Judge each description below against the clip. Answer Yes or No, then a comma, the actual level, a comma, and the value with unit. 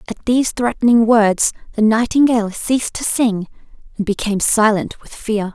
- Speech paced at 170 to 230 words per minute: No, average, 150 wpm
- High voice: Yes, high, 220 Hz